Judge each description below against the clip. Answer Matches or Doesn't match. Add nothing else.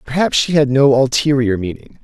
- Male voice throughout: Matches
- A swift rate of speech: Doesn't match